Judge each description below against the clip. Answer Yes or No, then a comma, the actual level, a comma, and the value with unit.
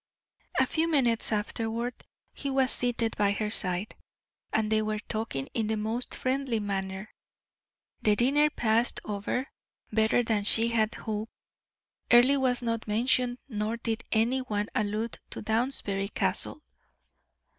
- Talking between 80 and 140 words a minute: Yes, slow, 135 wpm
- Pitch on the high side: Yes, high, 225 Hz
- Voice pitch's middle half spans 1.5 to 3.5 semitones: Yes, narrow, 2.5 semitones